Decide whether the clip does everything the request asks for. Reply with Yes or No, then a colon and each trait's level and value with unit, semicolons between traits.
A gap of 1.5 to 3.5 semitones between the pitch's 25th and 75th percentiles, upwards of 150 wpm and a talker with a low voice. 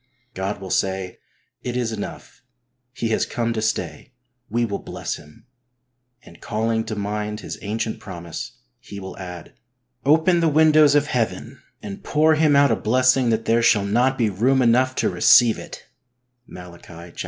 No: average, 4.3 semitones; average, 175 wpm; low, 115 Hz